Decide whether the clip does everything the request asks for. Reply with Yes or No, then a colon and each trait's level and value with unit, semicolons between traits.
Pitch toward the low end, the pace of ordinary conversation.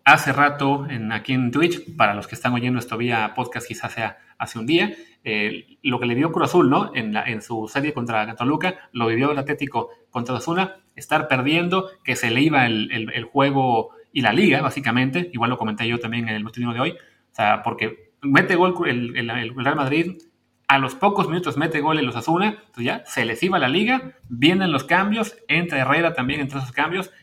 No: low, 130 Hz; fast, 220 wpm